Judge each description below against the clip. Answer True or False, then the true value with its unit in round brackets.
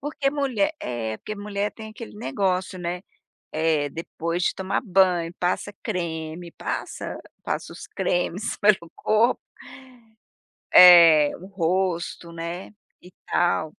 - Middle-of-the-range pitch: True (180 Hz)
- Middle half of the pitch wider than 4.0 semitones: False (3.5 semitones)